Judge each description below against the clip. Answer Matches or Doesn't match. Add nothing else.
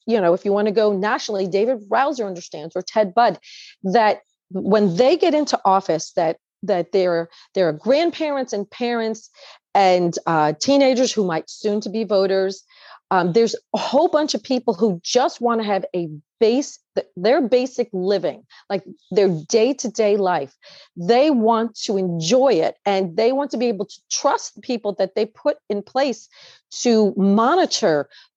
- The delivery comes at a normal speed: Matches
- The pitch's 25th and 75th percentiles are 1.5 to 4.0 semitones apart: Doesn't match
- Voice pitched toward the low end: Doesn't match